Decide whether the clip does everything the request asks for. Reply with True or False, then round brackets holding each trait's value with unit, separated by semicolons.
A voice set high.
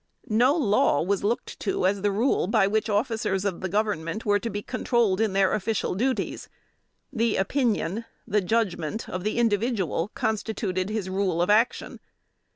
True (205 Hz)